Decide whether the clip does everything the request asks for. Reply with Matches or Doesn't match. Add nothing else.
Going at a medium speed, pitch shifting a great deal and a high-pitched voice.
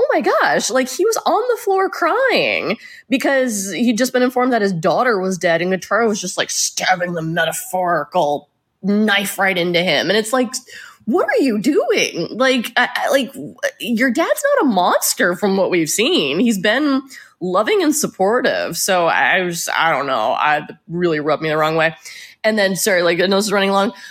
Matches